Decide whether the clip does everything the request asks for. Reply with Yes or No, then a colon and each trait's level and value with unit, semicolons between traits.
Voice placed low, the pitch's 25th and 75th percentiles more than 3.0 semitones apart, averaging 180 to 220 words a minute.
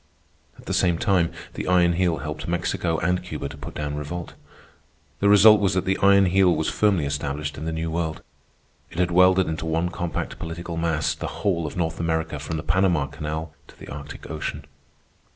No: very low, 80 Hz; average, 2.7 semitones; average, 195 wpm